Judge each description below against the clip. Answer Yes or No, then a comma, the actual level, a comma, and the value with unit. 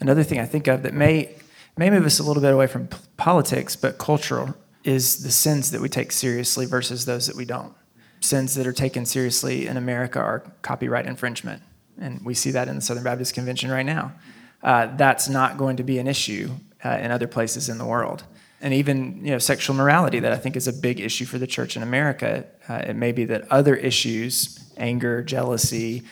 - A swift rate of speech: Yes, fast, 215 wpm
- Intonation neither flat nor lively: No, narrow, 1.8 semitones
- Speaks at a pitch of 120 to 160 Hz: Yes, low, 130 Hz